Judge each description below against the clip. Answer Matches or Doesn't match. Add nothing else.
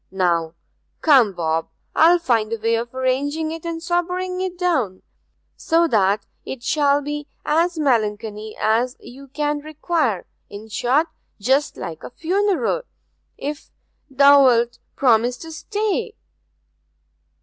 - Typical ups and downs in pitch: Doesn't match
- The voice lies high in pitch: Matches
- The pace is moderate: Doesn't match